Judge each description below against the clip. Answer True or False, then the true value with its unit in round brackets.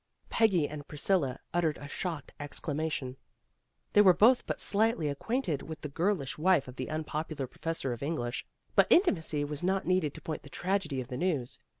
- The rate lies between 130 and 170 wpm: False (195 wpm)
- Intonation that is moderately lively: True (4.5 semitones)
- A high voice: False (155 Hz)